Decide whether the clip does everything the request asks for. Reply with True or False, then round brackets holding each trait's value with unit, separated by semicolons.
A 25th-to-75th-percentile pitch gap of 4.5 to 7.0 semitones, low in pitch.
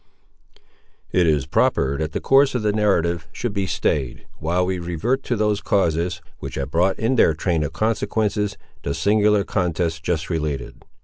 True (4.8 semitones; 90 Hz)